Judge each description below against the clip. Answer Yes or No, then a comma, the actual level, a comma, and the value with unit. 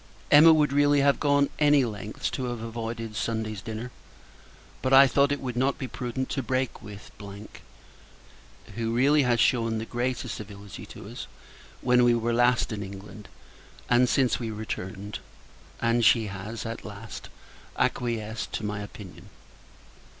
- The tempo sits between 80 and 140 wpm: No, average, 150 wpm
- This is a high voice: No, low, 115 Hz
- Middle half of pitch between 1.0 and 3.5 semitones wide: Yes, average, 3.2 semitones